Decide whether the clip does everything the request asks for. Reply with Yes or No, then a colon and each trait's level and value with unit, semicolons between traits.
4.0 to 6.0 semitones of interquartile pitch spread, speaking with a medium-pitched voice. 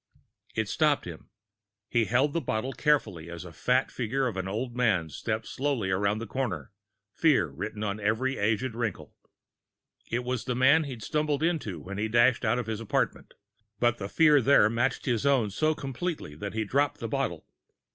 No: average, 4.4 semitones; low, 120 Hz